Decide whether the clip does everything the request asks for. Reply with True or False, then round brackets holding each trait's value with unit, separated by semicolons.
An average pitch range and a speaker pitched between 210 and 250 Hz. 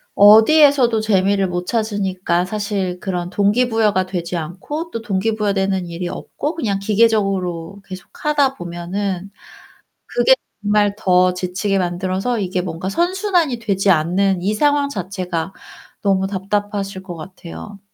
False (3.1 semitones; 195 Hz)